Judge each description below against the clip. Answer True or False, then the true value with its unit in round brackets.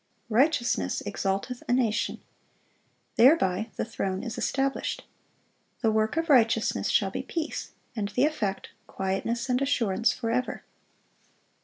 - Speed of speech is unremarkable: False (120 wpm)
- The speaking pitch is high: True (230 Hz)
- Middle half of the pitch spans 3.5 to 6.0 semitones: True (3.9 semitones)